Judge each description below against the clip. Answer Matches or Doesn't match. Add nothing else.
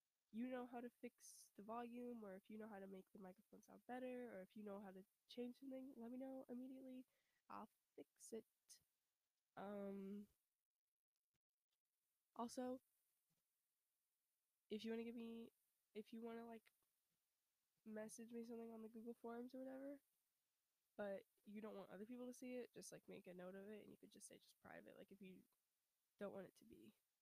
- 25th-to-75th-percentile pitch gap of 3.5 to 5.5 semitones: Doesn't match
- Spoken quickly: Doesn't match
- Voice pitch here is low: Doesn't match